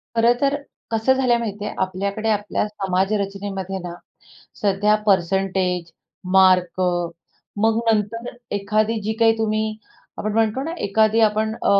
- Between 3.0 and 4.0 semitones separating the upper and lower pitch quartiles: No, narrow, 2.4 semitones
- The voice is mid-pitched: No, high, 210 Hz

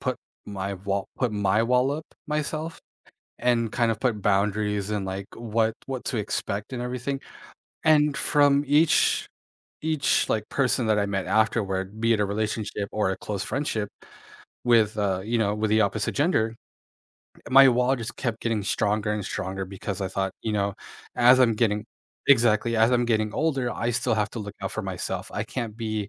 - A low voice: Yes, low, 110 Hz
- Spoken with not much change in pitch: No, average, 3.3 semitones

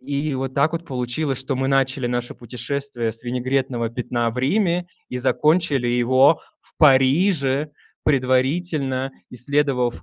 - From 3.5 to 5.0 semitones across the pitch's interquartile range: No, average, 2.7 semitones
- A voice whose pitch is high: No, low, 135 Hz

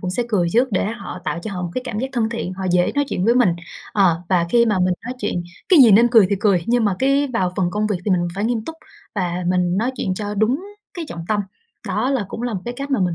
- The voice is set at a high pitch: Yes, high, 210 Hz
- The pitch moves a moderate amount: Yes, average, 4.8 semitones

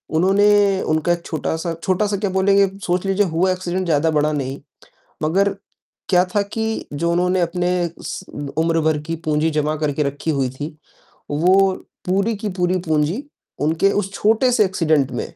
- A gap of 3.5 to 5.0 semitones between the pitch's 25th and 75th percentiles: Yes, average, 3.9 semitones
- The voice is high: No, medium, 175 Hz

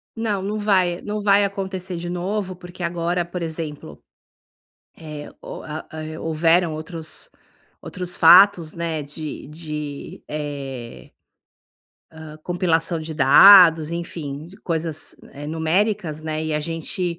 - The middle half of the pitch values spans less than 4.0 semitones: Yes, average, 2.8 semitones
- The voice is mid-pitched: Yes, medium, 165 Hz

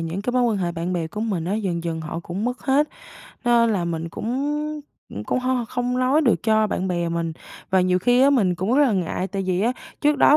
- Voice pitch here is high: Yes, high, 210 Hz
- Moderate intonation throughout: No, wide, 6.1 semitones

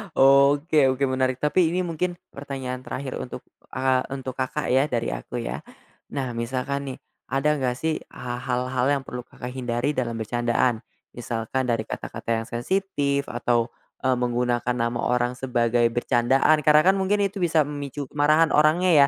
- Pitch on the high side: No, low, 130 Hz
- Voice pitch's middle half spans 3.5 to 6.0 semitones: No, average, 3.1 semitones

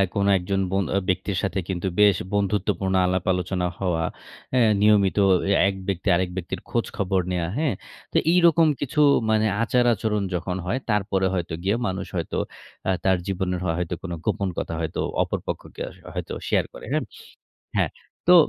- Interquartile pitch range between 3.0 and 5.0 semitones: No, narrow, 2.5 semitones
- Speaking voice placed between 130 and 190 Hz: No, very low, 95 Hz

